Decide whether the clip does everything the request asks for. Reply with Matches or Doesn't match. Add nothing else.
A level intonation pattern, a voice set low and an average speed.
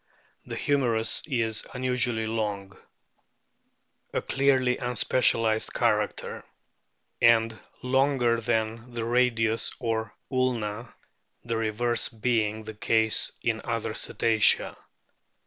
Doesn't match